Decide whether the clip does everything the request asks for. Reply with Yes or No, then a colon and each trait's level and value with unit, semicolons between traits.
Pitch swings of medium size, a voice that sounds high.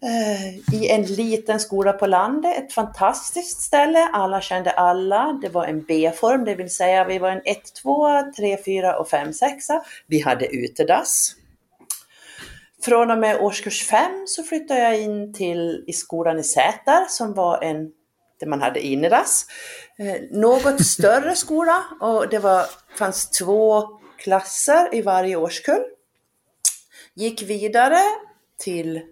No: wide, 7.0 semitones; high, 210 Hz